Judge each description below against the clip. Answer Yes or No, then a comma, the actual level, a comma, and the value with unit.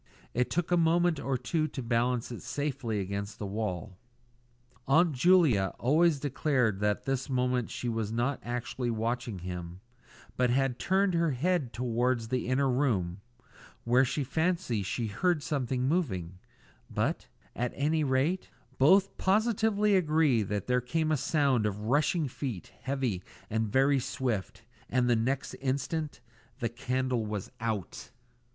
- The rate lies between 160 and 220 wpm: No, average, 145 wpm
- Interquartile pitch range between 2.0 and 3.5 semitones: No, average, 5.0 semitones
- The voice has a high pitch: No, low, 125 Hz